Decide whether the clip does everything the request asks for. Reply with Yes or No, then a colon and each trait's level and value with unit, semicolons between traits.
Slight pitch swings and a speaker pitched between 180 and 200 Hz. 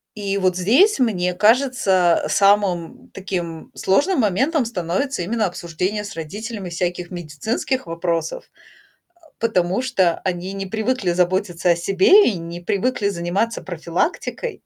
No: average, 4.3 semitones; high, 190 Hz